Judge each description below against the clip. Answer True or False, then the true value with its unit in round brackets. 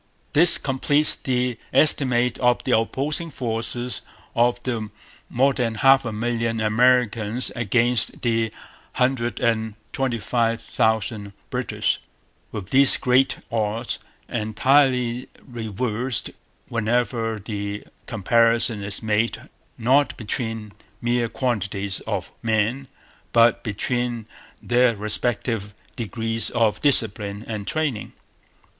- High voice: False (115 Hz)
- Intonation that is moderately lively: False (2.3 semitones)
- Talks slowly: True (105 wpm)